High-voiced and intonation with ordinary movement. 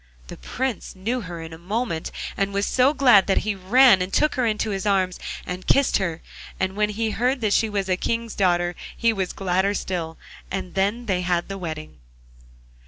Yes: high, 195 Hz; average, 3.9 semitones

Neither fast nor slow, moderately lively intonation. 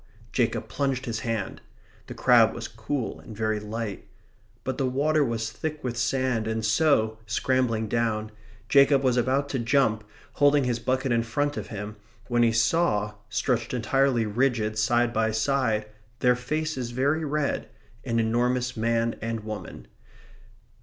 Yes: average, 150 wpm; average, 3.1 semitones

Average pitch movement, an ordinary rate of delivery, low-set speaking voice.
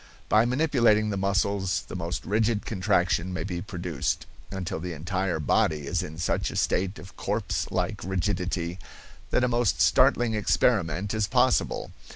Yes: average, 3.3 semitones; average, 155 wpm; very low, 95 Hz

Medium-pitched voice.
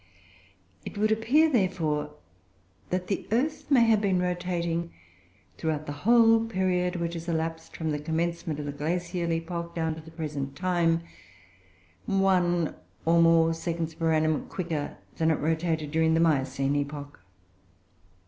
Yes: medium, 165 Hz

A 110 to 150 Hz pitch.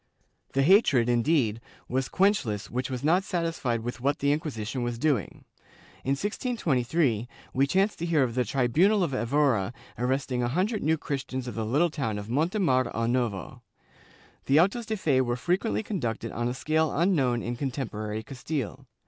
Yes: low, 135 Hz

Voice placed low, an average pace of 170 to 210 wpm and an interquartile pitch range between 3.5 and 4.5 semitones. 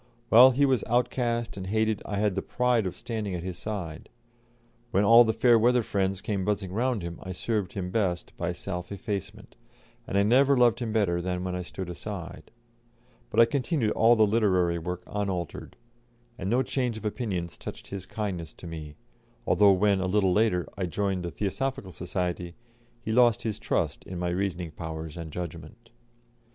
Yes: low, 100 Hz; average, 185 wpm; average, 4.2 semitones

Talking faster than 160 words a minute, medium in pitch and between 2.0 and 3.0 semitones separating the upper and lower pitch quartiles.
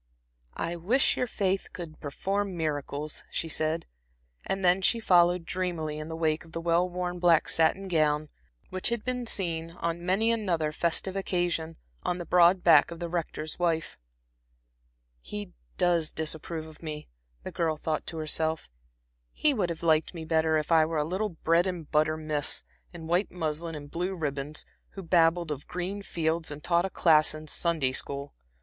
Yes: average, 175 wpm; medium, 165 Hz; narrow, 2.4 semitones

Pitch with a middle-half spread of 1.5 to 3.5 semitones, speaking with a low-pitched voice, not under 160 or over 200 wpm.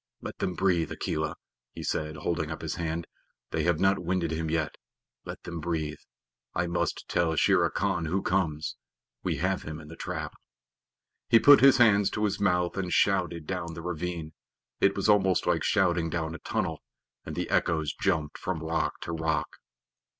Yes: average, 2.8 semitones; very low, 85 Hz; average, 180 wpm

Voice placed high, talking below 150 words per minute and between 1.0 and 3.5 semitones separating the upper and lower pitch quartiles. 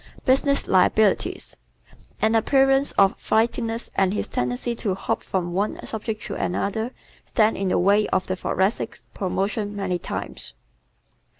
Yes: high, 205 Hz; average, 140 wpm; average, 3.0 semitones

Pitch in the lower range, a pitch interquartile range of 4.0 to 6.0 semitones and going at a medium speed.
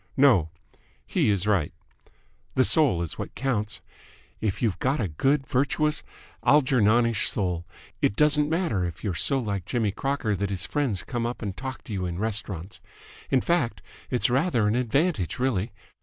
Yes: low, 115 Hz; wide, 5.4 semitones; average, 165 wpm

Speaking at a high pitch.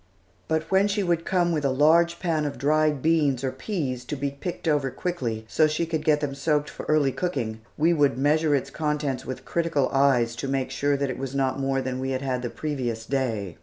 No: medium, 140 Hz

